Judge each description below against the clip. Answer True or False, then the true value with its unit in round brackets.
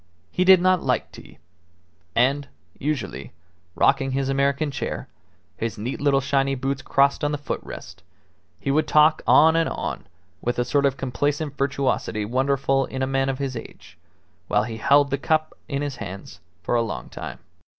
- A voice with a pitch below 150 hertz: True (135 Hz)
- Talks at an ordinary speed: True (175 wpm)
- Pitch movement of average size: False (2.0 semitones)